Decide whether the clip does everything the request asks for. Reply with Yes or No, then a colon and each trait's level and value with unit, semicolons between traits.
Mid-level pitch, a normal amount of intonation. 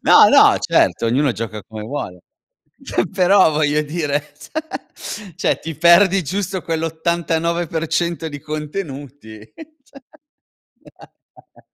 Yes: medium, 160 Hz; average, 3.4 semitones